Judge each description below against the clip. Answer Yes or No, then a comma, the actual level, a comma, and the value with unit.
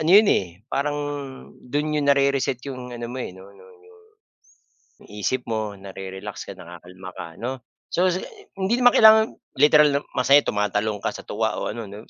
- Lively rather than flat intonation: Yes, wide, 6.4 semitones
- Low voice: Yes, low, 125 Hz